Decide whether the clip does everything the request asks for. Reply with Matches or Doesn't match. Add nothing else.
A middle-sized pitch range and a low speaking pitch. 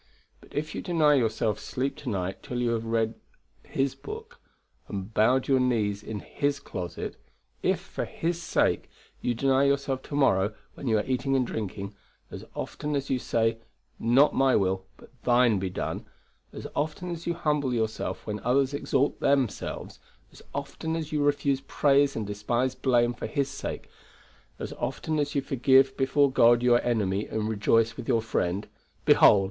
Matches